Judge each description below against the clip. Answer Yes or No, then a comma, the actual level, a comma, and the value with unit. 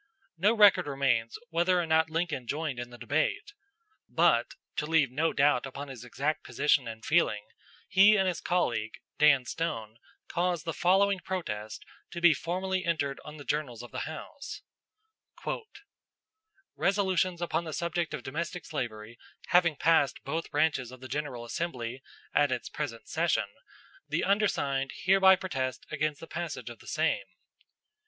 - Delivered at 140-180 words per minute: Yes, average, 150 wpm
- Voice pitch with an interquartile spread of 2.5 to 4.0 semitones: No, average, 5.1 semitones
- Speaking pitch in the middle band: Yes, medium, 155 Hz